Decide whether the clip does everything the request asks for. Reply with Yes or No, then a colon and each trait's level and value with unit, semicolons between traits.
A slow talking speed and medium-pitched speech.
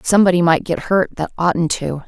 No: average, 200 wpm; medium, 175 Hz